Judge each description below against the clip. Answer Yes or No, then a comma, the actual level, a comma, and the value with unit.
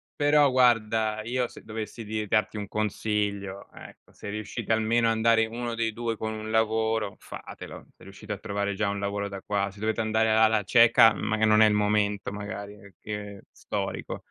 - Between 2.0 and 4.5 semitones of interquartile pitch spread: No, narrow, 1.5 semitones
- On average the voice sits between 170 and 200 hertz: No, low, 110 Hz